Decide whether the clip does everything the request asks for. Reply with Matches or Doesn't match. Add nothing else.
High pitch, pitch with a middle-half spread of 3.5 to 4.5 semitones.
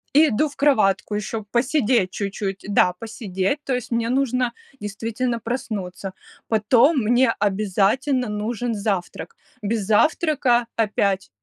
Matches